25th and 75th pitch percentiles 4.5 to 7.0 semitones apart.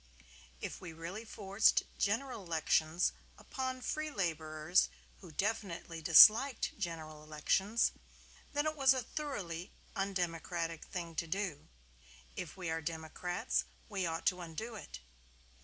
Yes: average, 4.9 semitones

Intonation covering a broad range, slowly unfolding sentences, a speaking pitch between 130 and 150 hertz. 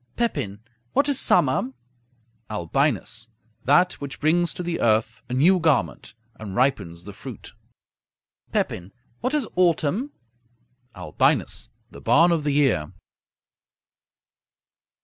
Yes: wide, 8.2 semitones; slow, 110 wpm; medium, 140 Hz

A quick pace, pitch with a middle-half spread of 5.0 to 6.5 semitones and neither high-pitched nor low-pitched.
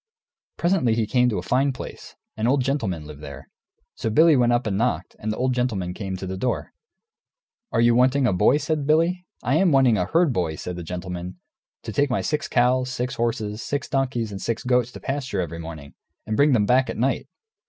No: fast, 215 wpm; wide, 5.6 semitones; low, 120 Hz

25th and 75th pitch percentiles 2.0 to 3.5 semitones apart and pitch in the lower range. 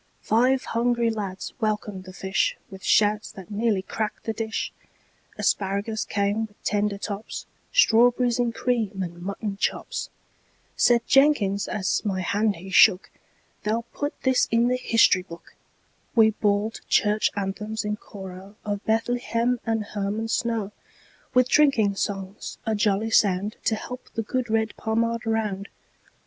No: narrow, 2.5 semitones; high, 215 Hz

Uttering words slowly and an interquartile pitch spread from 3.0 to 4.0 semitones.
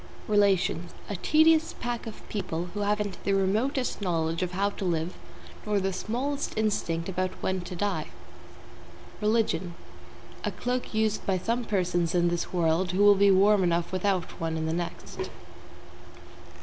No: average, 155 wpm; average, 3.3 semitones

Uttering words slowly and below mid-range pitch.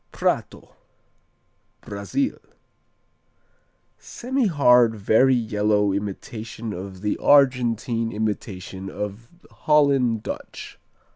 Yes: slow, 70 wpm; low, 115 Hz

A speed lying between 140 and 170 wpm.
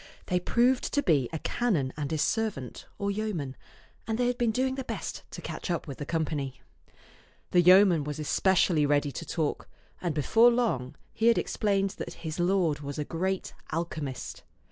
No: average, 180 wpm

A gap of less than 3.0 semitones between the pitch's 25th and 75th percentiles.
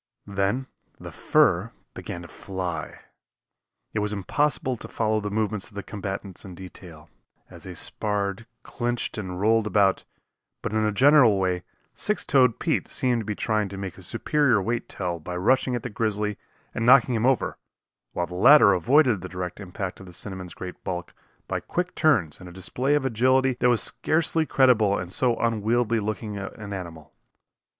No: average, 4.5 semitones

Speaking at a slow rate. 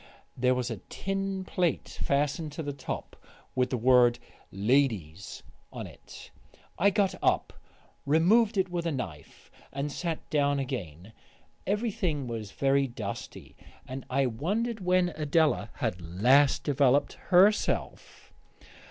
Yes: slow, 125 wpm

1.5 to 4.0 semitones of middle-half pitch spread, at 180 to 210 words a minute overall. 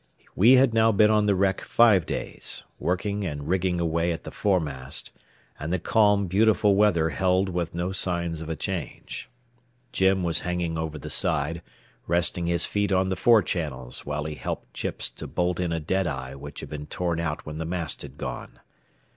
Yes: average, 3.2 semitones; average, 190 wpm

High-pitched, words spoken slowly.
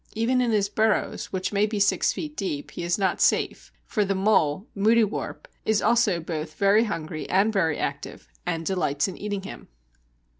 No: high, 200 Hz; average, 180 wpm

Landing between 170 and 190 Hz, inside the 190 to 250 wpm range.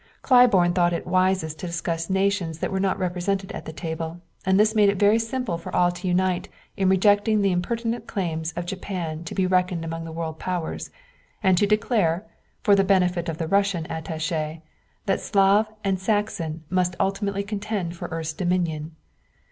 No: medium, 185 Hz; average, 180 wpm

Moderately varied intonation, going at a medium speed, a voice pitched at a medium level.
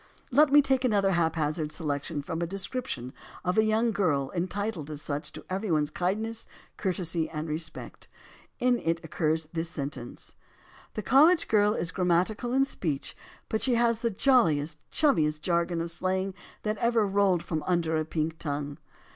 No: wide, 5.7 semitones; average, 165 wpm; medium, 175 Hz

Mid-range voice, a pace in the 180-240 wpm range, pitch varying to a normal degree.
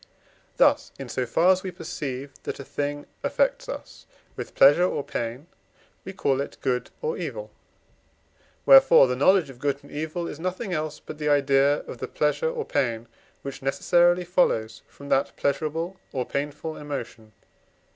No: medium, 145 Hz; average, 165 wpm; average, 4.5 semitones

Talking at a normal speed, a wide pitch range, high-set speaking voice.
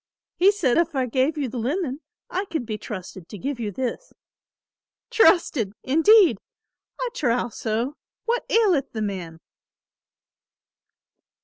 No: slow, 130 wpm; wide, 7.6 semitones; very high, 265 Hz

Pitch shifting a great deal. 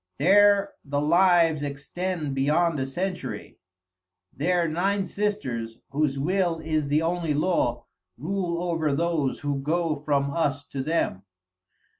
No: average, 3.8 semitones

